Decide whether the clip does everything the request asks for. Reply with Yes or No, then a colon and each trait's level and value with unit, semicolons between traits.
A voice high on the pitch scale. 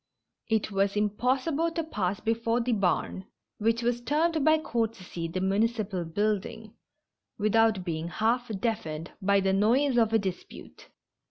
Yes: high, 220 Hz